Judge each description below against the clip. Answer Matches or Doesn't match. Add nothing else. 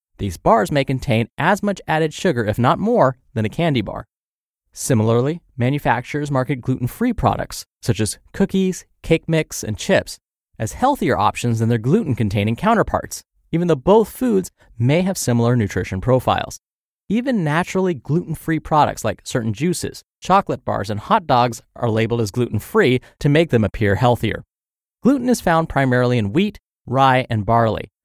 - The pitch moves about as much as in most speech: Doesn't match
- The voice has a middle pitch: Doesn't match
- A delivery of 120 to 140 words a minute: Doesn't match